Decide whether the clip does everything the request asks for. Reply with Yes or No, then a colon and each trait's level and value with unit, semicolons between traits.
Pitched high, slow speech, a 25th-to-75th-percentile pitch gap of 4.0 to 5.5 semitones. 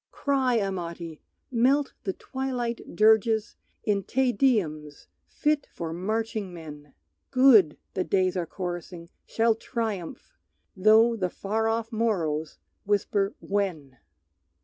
Yes: high, 205 Hz; slow, 110 wpm; average, 4.8 semitones